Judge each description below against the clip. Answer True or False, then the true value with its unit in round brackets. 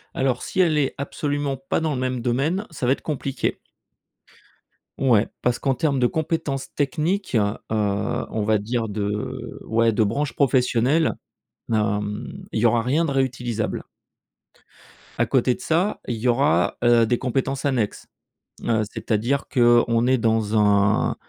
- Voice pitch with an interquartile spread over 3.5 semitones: True (3.9 semitones)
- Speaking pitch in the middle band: False (125 Hz)